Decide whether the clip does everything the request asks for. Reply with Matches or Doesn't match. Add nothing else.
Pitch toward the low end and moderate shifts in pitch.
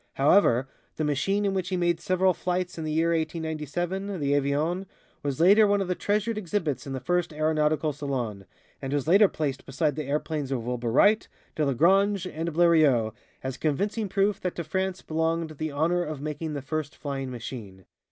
Doesn't match